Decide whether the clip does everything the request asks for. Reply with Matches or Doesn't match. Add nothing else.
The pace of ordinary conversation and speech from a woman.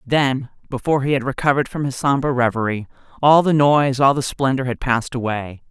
Matches